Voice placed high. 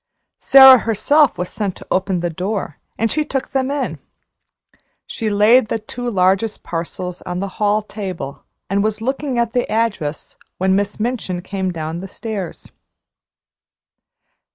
Yes: high, 205 Hz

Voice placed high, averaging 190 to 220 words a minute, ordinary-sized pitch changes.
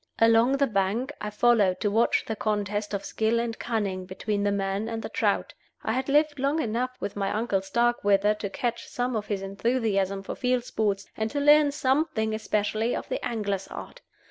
Yes: high, 220 Hz; average, 195 wpm; average, 3.3 semitones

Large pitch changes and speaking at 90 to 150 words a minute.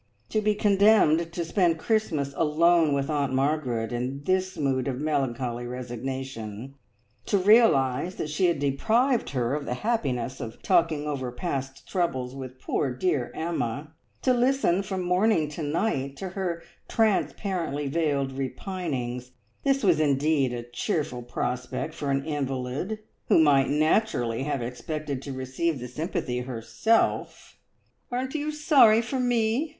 Yes: wide, 6.2 semitones; average, 140 wpm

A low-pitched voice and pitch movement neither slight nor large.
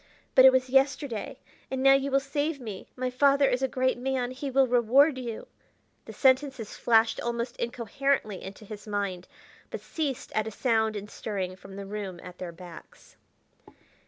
No: high, 245 Hz; average, 4.3 semitones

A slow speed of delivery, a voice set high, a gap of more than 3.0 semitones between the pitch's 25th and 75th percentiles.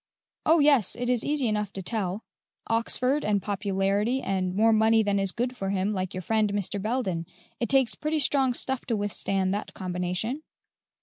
No: average, 180 wpm; high, 210 Hz; average, 4.2 semitones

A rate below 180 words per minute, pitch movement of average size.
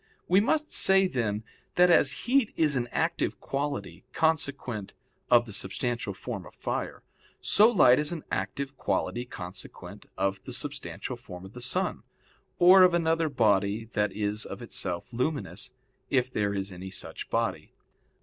No: average, 155 wpm; wide, 7.6 semitones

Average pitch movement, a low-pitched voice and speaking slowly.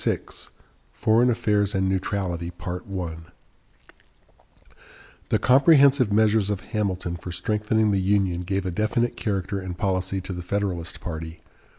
Yes: average, 3.1 semitones; low, 100 Hz; slow, 120 wpm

